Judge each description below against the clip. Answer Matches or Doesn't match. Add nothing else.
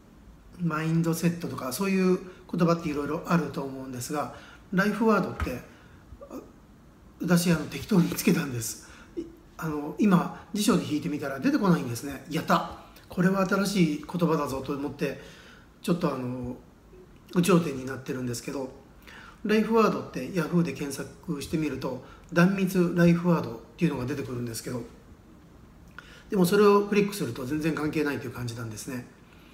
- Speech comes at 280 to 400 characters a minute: Matches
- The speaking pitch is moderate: Matches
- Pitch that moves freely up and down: Doesn't match